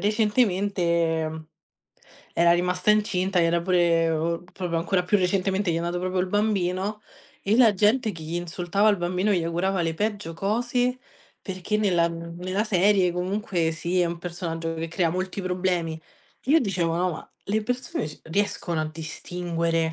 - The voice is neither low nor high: Yes, medium, 180 Hz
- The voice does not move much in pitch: No, average, 3.2 semitones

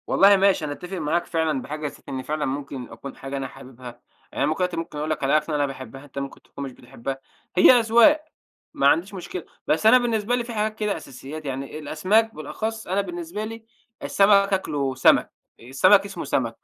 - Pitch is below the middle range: No, medium, 155 Hz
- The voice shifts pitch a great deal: Yes, wide, 6.4 semitones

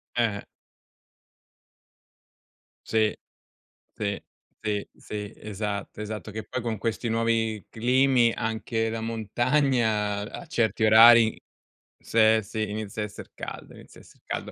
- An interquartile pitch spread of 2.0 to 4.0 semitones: No, narrow, 1.4 semitones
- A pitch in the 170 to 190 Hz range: No, low, 110 Hz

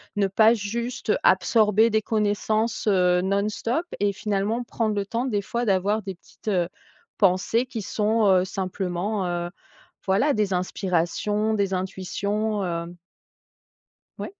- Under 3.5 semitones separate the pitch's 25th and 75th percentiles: Yes, average, 2.7 semitones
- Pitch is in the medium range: No, high, 205 Hz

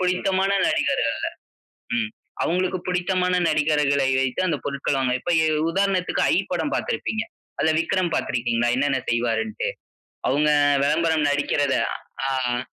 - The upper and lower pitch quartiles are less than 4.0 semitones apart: No, average, 4.9 semitones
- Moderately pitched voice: Yes, medium, 155 Hz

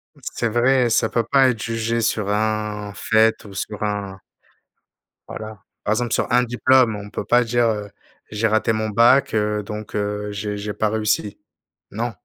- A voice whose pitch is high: No, low, 110 Hz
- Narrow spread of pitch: Yes, narrow, 2.0 semitones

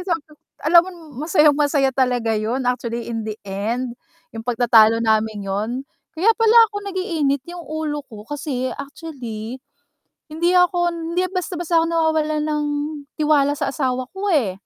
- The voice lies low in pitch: No, very high, 290 Hz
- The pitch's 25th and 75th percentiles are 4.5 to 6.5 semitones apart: Yes, wide, 5.6 semitones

